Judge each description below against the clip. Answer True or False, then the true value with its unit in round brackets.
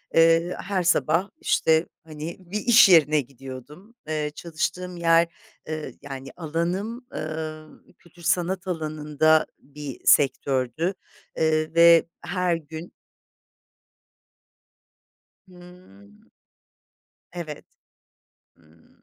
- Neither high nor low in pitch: True (160 Hz)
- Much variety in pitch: False (2.9 semitones)